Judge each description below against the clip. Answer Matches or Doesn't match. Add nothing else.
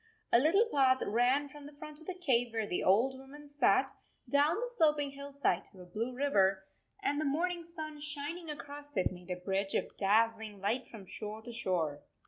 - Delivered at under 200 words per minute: Doesn't match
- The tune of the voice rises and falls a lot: Matches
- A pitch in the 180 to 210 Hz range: Doesn't match